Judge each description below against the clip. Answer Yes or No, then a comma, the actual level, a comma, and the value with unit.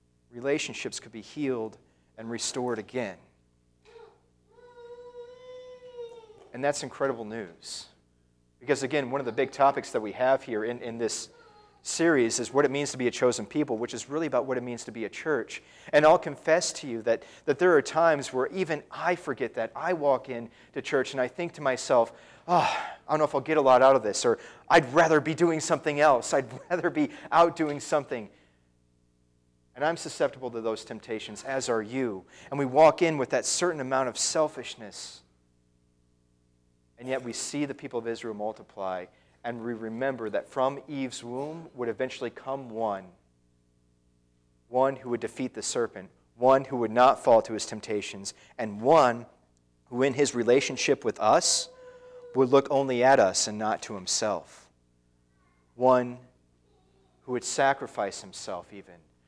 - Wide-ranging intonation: Yes, wide, 6.6 semitones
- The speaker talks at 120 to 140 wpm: No, average, 175 wpm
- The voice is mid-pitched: No, low, 125 Hz